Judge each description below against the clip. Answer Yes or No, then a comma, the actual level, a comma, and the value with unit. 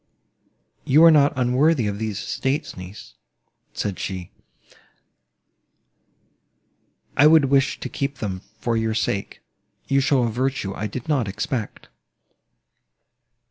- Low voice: Yes, low, 120 Hz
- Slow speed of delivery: Yes, slow, 115 wpm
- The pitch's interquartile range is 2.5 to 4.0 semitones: No, average, 5.1 semitones